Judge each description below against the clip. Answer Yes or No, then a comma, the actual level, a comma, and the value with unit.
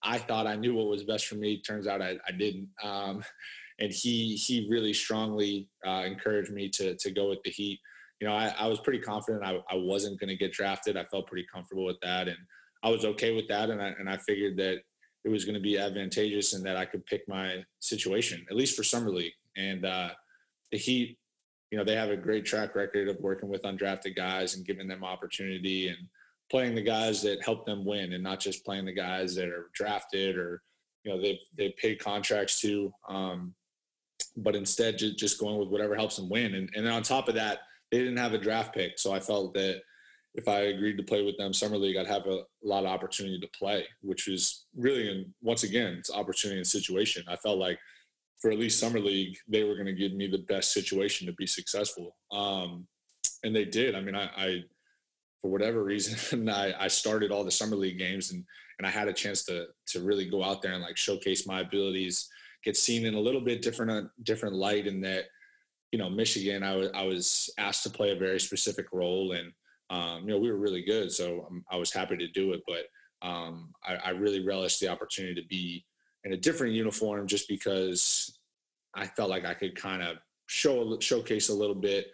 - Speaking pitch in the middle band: No, low, 100 Hz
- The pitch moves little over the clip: Yes, narrow, 2.0 semitones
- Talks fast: Yes, fast, 220 wpm